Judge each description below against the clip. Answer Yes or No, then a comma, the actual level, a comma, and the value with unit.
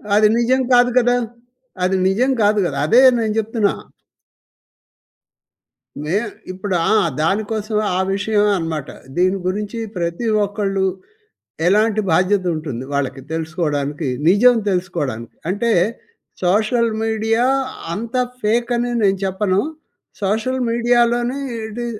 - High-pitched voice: Yes, high, 210 Hz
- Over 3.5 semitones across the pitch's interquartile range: Yes, average, 4.0 semitones